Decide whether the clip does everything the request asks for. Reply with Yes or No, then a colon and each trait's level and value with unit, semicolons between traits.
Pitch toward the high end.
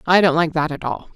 No: medium, 165 Hz